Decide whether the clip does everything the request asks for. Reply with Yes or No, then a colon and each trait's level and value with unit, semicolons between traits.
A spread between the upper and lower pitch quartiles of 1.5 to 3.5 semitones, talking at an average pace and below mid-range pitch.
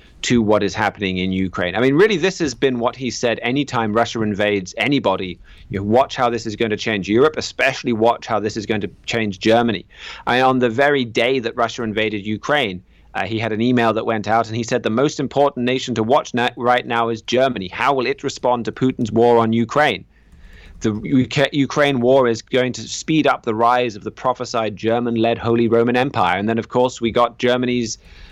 No: narrow, 2.5 semitones; fast, 215 wpm; low, 115 Hz